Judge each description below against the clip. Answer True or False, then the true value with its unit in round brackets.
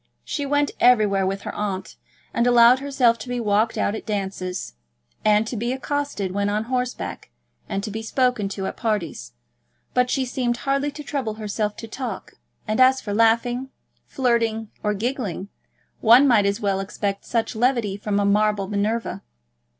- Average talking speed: True (170 wpm)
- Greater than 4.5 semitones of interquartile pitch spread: False (3.6 semitones)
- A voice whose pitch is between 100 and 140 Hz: False (225 Hz)